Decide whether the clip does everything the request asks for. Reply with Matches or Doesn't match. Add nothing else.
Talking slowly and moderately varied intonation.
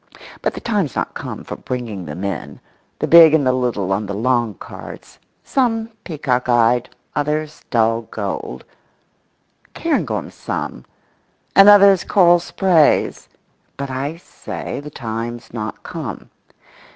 Doesn't match